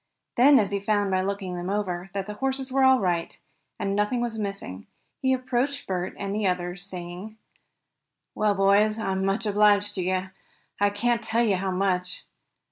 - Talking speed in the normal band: Yes, average, 185 wpm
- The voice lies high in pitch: Yes, high, 200 Hz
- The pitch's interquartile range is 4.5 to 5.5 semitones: No, average, 2.8 semitones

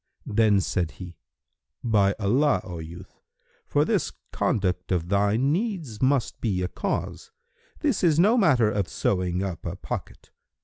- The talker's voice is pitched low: Yes, low, 105 Hz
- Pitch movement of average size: No, wide, 7.2 semitones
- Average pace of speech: Yes, average, 145 wpm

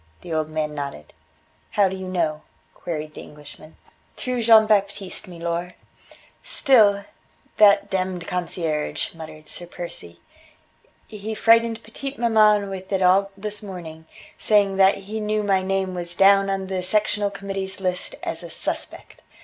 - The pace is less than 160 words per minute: Yes, average, 145 wpm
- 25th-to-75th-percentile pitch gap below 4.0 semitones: Yes, average, 3.3 semitones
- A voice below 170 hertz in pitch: No, high, 190 Hz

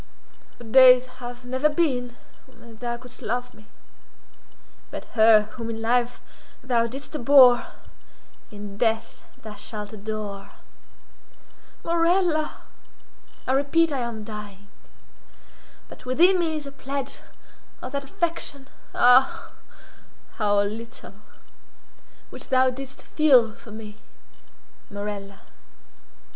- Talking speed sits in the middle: No, slow, 105 wpm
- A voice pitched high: Yes, high, 245 Hz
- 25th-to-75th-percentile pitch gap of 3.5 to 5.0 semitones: Yes, average, 4.0 semitones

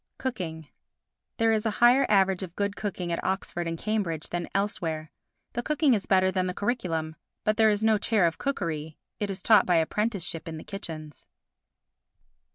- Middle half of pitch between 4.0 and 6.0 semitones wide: Yes, average, 4.5 semitones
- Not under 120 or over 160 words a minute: No, average, 175 wpm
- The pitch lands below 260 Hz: Yes, high, 190 Hz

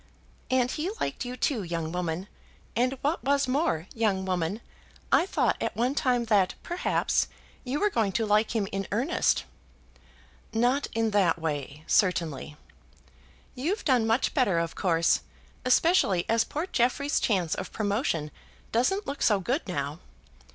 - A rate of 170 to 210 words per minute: No, average, 150 wpm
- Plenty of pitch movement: Yes, wide, 6.4 semitones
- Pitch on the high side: Yes, high, 225 Hz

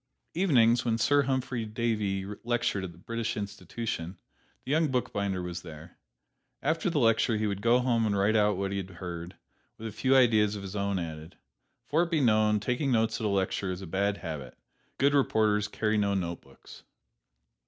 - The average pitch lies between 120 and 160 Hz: No, low, 105 Hz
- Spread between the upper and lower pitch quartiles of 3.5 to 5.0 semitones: Yes, average, 3.8 semitones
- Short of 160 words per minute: No, average, 185 wpm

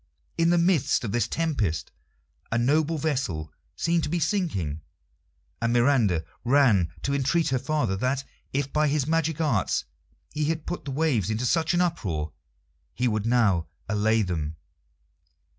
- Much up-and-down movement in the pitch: Yes, wide, 7.0 semitones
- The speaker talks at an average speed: Yes, average, 155 wpm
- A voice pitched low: Yes, low, 130 Hz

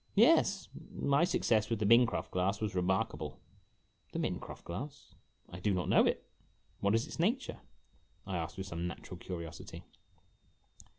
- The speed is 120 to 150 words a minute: Yes, average, 140 wpm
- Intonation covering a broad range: Yes, wide, 7.3 semitones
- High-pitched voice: No, low, 100 Hz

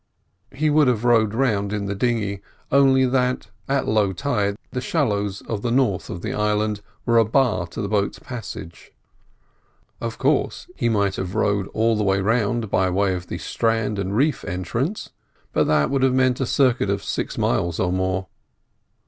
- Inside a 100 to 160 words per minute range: No, average, 180 wpm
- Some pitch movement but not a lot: Yes, average, 4.2 semitones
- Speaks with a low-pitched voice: Yes, low, 110 Hz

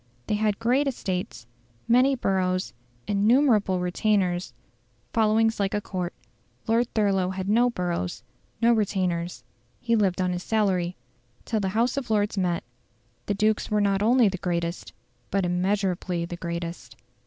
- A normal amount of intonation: Yes, average, 3.4 semitones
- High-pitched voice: Yes, high, 200 Hz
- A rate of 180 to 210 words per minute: No, average, 145 wpm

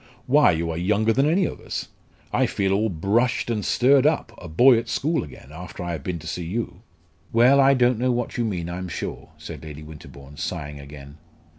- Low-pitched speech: Yes, low, 100 Hz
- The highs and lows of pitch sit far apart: Yes, wide, 7.4 semitones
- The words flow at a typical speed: No, fast, 210 wpm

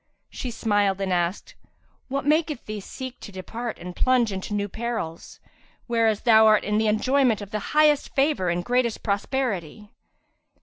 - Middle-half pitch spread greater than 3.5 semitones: Yes, average, 4.2 semitones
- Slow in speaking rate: No, average, 160 wpm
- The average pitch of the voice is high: Yes, high, 220 Hz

